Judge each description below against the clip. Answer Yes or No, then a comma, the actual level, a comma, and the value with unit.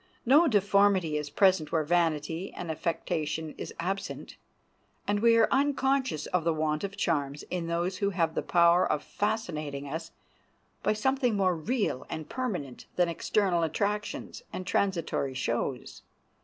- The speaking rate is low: No, average, 145 wpm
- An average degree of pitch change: Yes, average, 4.6 semitones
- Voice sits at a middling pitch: Yes, medium, 175 Hz